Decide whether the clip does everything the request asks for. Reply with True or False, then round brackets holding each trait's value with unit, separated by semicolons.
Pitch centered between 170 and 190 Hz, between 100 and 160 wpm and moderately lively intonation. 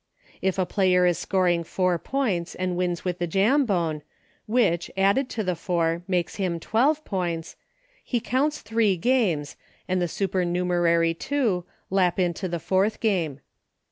True (185 Hz; 145 wpm; 3.4 semitones)